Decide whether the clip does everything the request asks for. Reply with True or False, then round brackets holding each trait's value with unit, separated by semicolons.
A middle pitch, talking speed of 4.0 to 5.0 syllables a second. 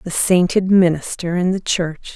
True (175 Hz; 4.4 syllables/s)